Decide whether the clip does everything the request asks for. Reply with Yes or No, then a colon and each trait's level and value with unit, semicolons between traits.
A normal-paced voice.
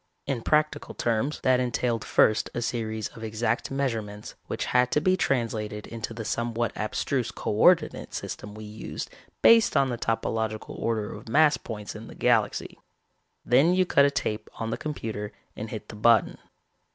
Yes: average, 170 wpm